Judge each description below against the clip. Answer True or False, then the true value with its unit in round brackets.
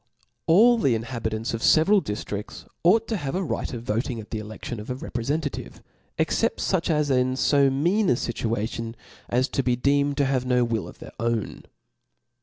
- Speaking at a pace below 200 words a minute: False (205 wpm)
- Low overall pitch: True (125 Hz)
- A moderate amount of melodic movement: True (4.6 semitones)